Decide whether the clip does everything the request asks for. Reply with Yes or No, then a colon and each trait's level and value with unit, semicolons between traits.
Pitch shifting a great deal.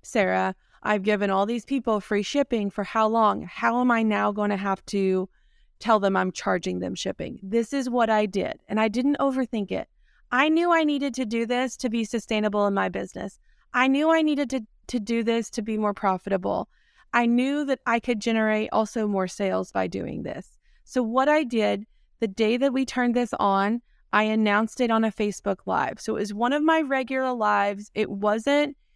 No: average, 3.6 semitones